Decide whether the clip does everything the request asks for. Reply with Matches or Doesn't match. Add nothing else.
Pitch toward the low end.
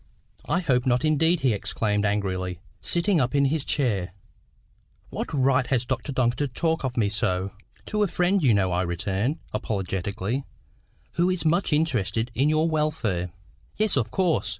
Matches